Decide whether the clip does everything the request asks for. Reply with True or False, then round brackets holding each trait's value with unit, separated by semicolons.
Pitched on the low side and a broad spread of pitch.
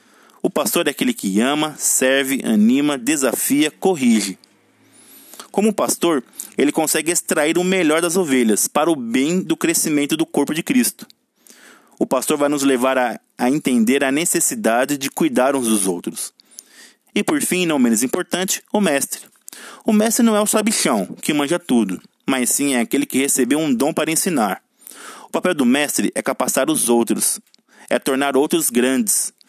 False (160 Hz; 8.6 semitones)